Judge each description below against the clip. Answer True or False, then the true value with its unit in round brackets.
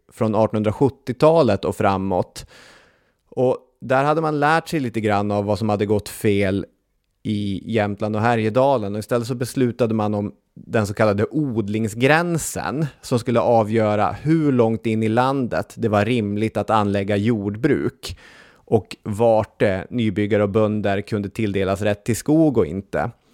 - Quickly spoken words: False (150 wpm)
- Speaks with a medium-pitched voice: False (110 Hz)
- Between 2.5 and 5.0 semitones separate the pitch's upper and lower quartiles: True (3.2 semitones)